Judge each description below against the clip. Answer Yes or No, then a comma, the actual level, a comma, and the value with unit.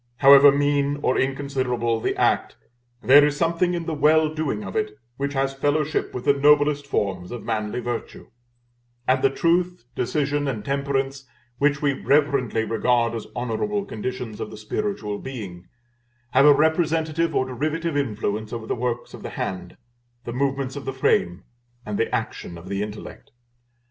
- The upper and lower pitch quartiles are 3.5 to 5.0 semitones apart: Yes, average, 4.2 semitones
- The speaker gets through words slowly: No, average, 165 wpm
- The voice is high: No, low, 135 Hz